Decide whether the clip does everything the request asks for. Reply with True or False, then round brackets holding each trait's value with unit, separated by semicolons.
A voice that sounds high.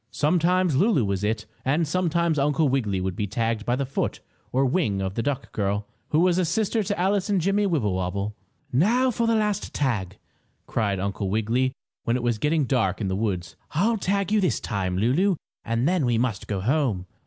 False (130 Hz)